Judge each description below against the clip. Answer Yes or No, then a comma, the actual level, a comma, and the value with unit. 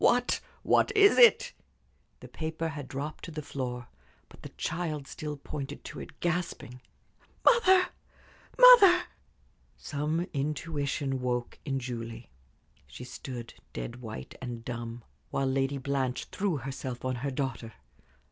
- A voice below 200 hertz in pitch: Yes, medium, 140 Hz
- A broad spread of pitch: No, average, 4.4 semitones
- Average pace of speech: No, slow, 130 wpm